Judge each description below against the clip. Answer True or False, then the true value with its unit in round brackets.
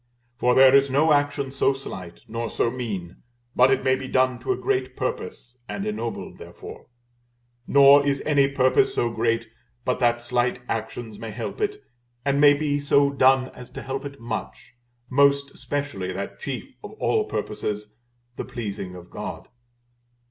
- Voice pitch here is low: True (130 Hz)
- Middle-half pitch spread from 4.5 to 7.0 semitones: False (3.4 semitones)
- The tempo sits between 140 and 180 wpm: True (165 wpm)